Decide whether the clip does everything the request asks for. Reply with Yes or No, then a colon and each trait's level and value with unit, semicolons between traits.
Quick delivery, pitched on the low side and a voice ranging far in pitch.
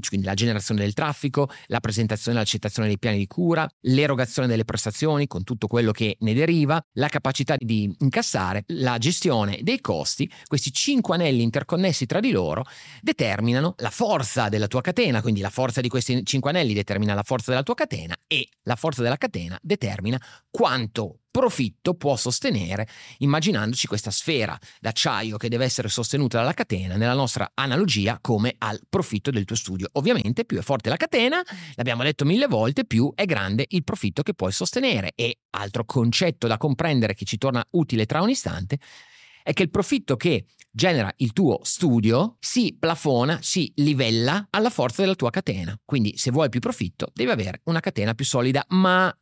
Yes: fast, 175 wpm; low, 130 Hz; wide, 6.1 semitones